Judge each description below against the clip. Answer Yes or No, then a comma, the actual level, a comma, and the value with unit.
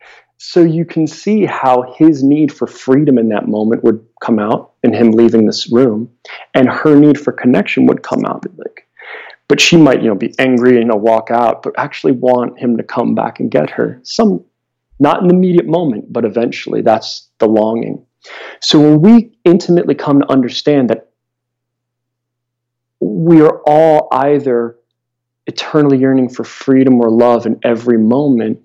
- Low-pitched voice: Yes, low, 125 Hz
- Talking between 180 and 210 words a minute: No, average, 170 wpm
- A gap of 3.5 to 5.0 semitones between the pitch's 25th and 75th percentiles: Yes, average, 3.9 semitones